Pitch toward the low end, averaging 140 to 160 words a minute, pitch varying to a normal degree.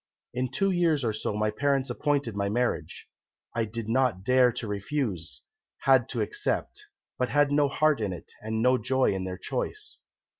No: low, 125 Hz; average, 180 wpm; average, 4.5 semitones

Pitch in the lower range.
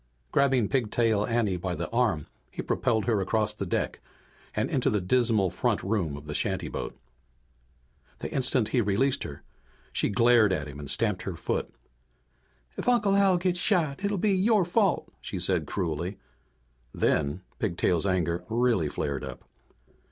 Yes: low, 110 Hz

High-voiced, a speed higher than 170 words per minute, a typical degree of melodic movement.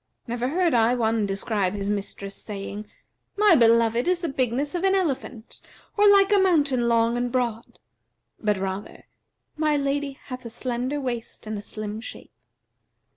No: high, 240 Hz; average, 160 wpm; average, 4.9 semitones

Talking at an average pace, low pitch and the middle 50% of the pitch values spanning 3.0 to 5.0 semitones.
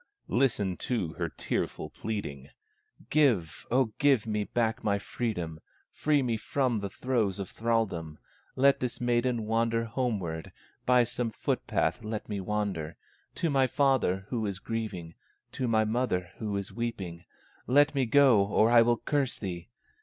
Yes: average, 155 wpm; low, 110 Hz; average, 4.0 semitones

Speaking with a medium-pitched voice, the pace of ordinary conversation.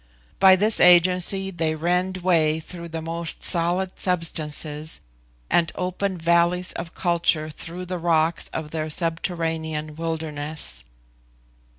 No: medium, 170 Hz; slow, 115 wpm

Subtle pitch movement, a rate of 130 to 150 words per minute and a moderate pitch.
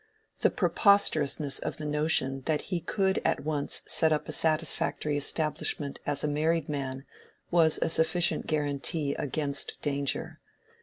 Yes: narrow, 2.1 semitones; average, 140 wpm; medium, 150 Hz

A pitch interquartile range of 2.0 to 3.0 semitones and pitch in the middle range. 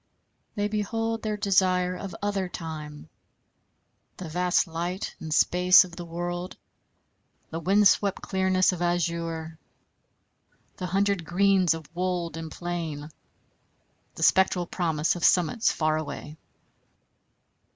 Yes: narrow, 2.5 semitones; medium, 180 Hz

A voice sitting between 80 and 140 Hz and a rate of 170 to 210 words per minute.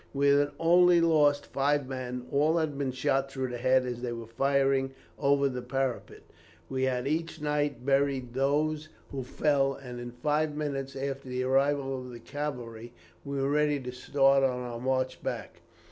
Yes: low, 135 Hz; average, 175 wpm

